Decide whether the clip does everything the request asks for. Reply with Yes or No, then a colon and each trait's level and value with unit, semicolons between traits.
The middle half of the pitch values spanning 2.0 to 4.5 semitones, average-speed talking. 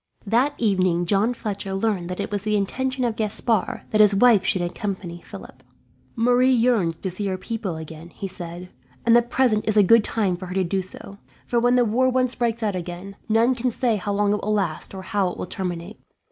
No: average, 3.9 semitones; fast, 220 wpm